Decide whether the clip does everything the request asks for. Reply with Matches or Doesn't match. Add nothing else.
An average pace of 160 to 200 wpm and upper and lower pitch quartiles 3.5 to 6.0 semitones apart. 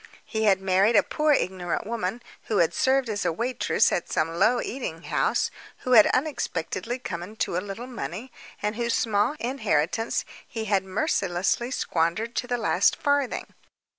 Matches